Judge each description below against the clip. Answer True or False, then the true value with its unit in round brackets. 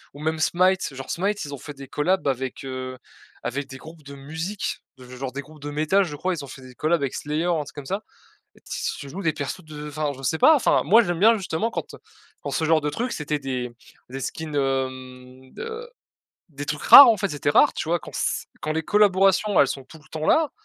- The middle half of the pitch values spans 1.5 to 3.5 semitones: False (5.1 semitones)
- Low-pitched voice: False (150 Hz)